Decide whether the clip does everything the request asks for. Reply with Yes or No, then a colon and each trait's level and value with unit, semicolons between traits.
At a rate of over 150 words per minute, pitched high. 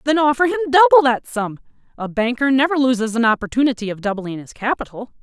Yes: average, 185 wpm; very high, 250 Hz